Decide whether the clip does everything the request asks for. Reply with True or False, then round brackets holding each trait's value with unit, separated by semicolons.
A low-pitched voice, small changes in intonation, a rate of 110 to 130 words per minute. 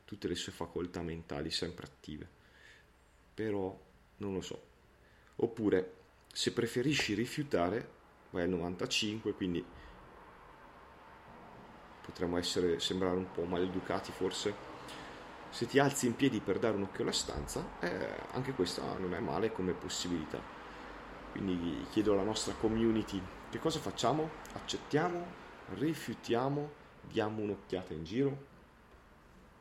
False (95 Hz; 4.6 semitones; 120 wpm)